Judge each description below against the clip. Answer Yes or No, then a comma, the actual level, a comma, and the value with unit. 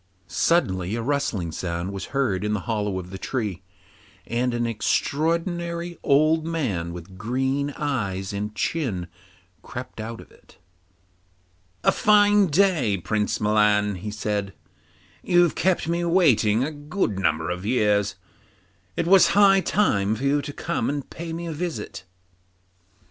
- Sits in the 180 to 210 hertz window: No, low, 120 Hz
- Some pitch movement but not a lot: No, wide, 8.3 semitones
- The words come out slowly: No, average, 145 wpm